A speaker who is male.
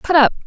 No: female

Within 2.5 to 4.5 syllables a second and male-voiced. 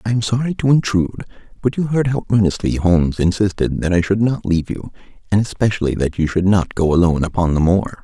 No: 6.3 syllables/s; male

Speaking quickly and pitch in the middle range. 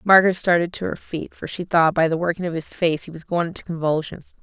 Yes: fast, 245 wpm; medium, 170 Hz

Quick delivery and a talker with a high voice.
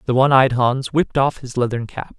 No: fast, 245 wpm; low, 130 Hz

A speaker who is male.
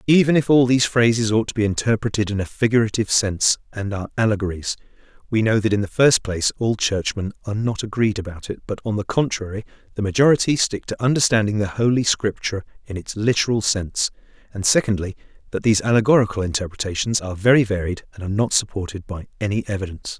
Yes: male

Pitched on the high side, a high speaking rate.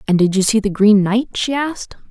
Yes: high, 215 Hz; fast, 255 wpm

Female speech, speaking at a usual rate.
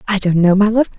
No: female; fast, 305 wpm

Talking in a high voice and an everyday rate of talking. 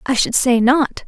No: very high, 255 Hz; fast, 225 wpm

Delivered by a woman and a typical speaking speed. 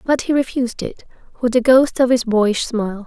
No: female; fast, 215 wpm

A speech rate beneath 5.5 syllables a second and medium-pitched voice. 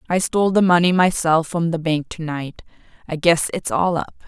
Yes: 5.2 syllables/s; medium, 170 Hz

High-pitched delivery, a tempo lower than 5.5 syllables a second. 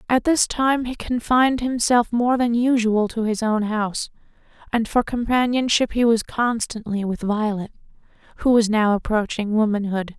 Yes: high, 230 Hz; 4.8 syllables/s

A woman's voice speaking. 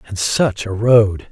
No: male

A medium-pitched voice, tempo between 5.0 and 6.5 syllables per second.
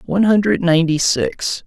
Yes: medium, 175 Hz; 5.3 syllables/s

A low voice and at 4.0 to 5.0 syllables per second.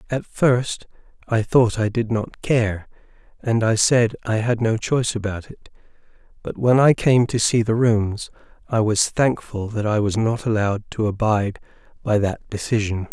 Yes: low, 110 Hz; 4.5 syllables/s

